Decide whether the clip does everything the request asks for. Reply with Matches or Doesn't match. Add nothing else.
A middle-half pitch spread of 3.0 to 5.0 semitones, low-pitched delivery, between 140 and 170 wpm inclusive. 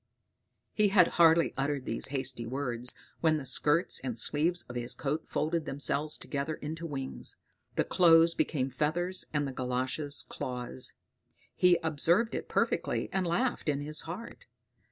Doesn't match